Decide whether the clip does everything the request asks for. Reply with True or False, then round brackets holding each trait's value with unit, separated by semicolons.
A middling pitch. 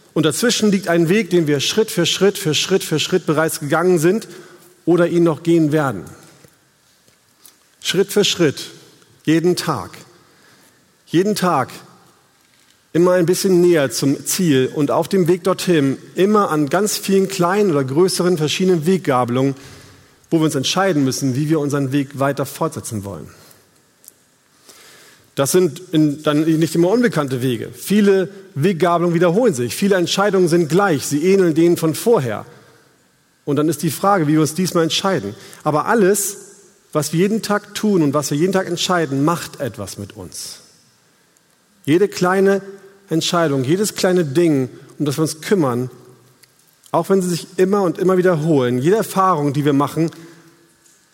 True (170 Hz)